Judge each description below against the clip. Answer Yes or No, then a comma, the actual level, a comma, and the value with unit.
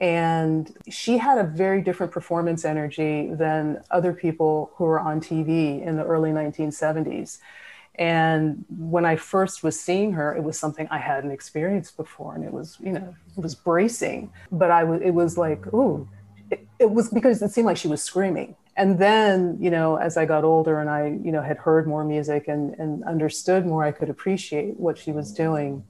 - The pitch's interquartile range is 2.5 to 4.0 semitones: Yes, average, 2.8 semitones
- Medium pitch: Yes, medium, 160 Hz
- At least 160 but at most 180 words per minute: No, average, 195 wpm